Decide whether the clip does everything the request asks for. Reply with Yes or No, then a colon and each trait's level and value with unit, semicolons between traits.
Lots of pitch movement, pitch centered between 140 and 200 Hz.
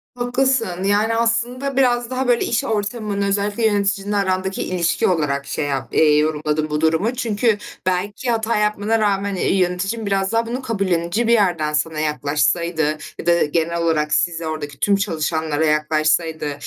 Yes: wide, 5.9 semitones; high, 190 Hz